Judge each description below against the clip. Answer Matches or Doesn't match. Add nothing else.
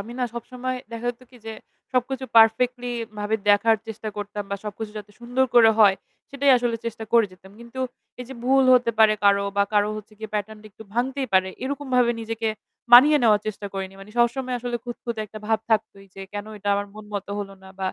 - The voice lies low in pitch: Doesn't match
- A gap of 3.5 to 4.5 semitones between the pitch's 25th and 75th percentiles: Doesn't match